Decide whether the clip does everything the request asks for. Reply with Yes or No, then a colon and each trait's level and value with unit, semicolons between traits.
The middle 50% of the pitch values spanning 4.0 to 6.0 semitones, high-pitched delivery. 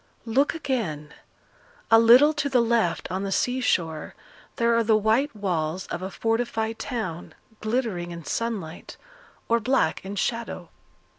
Yes: average, 4.5 semitones; high, 225 Hz